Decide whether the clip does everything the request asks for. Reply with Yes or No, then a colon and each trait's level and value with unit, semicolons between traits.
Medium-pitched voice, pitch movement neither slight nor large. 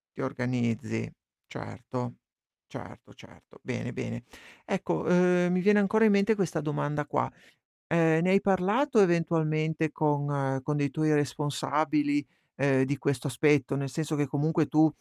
Yes: medium, 155 Hz; average, 4.2 semitones